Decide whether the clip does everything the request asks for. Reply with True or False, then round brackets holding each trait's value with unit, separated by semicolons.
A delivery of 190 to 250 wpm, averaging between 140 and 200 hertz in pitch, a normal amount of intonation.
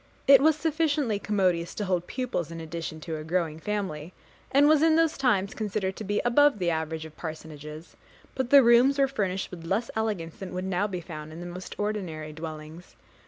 False (200 wpm; 185 Hz; 6.6 semitones)